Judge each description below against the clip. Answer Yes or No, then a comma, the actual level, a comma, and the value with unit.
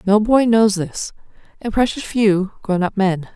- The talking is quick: No, average, 160 wpm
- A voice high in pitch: Yes, high, 205 Hz